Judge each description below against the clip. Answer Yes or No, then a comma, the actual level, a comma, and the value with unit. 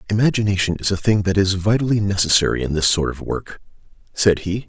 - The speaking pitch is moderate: No, low, 100 Hz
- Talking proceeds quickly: No, average, 190 wpm